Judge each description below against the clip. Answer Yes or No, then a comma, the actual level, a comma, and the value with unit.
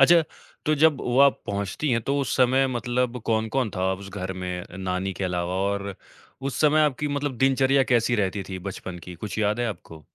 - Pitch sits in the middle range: No, low, 110 Hz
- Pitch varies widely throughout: Yes, wide, 6.0 semitones